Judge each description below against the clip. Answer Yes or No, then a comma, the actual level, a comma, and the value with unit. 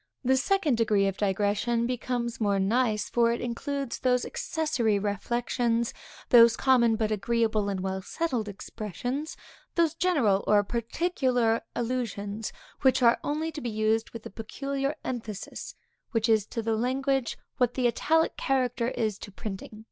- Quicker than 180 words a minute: No, average, 145 wpm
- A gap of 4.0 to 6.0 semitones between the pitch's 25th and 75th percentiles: No, average, 3.2 semitones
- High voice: Yes, high, 235 Hz